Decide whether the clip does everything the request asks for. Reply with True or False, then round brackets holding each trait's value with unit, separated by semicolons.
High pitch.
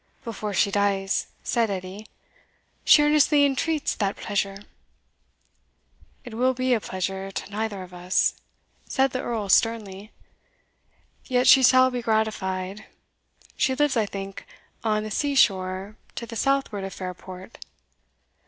True (215 Hz)